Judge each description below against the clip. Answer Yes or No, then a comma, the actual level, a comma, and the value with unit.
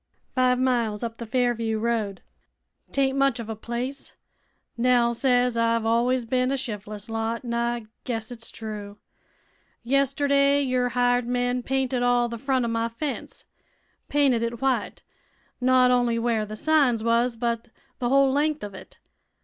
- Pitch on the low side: No, high, 245 Hz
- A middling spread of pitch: No, narrow, 2.0 semitones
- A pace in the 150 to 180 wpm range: Yes, average, 155 wpm